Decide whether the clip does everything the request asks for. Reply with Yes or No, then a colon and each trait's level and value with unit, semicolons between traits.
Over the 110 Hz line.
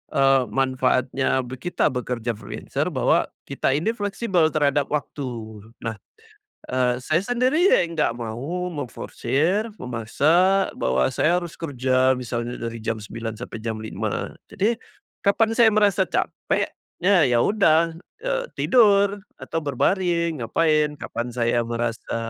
Yes: medium, 140 Hz